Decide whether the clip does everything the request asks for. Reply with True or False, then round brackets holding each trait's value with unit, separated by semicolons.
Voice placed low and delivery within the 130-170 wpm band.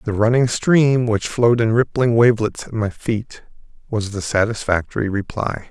True (115 Hz; 160 wpm)